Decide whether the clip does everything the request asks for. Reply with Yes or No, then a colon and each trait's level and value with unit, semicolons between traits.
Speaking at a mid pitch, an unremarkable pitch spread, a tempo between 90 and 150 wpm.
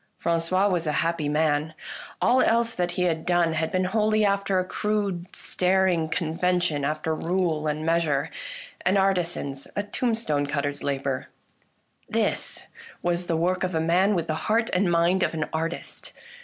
No: medium, 170 Hz; average, 3.0 semitones; average, 170 wpm